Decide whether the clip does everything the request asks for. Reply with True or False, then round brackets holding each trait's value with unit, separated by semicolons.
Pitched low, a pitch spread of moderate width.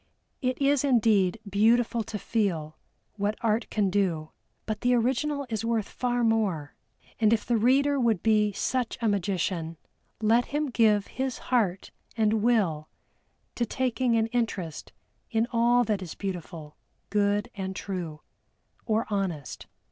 False (220 Hz; 3.8 semitones)